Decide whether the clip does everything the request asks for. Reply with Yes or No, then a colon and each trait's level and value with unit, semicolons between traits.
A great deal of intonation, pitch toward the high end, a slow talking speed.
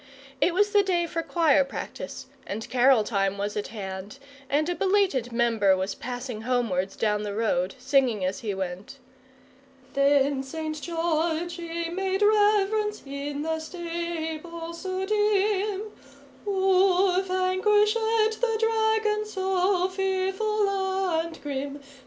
Yes: wide, 6.9 semitones; very high, 335 Hz; slow, 125 wpm